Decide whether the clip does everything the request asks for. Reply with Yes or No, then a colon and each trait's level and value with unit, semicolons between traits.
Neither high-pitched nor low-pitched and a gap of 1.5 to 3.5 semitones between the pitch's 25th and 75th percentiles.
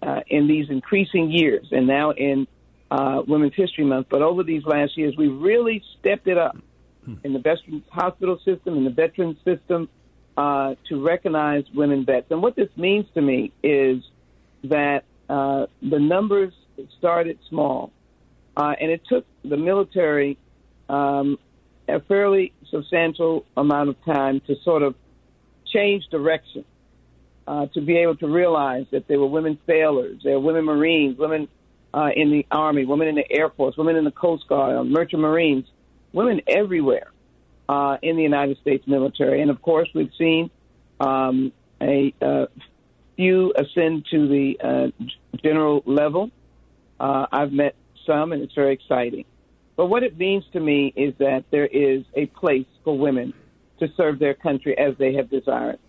Yes: medium, 145 Hz; average, 3.2 semitones